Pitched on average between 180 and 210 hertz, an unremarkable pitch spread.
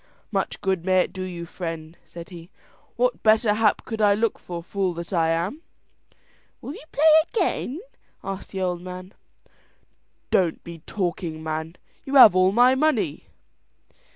Yes: medium, 185 Hz; average, 4.0 semitones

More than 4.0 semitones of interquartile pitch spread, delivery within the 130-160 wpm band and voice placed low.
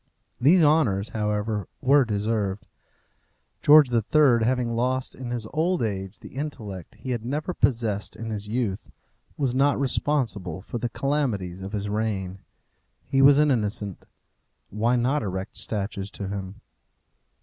Yes: average, 5.0 semitones; average, 140 wpm; low, 115 Hz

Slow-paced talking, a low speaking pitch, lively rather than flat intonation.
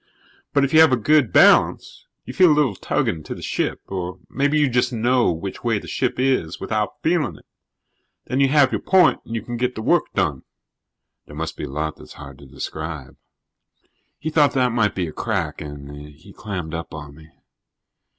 No: fast, 205 wpm; low, 110 Hz; wide, 9.0 semitones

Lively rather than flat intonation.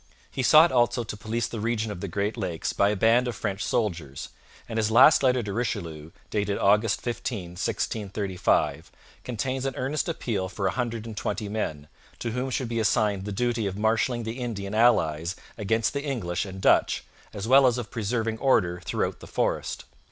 No: average, 3.5 semitones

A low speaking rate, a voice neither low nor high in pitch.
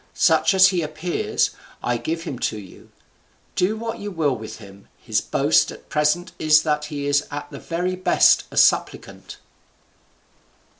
No: average, 160 wpm; medium, 155 Hz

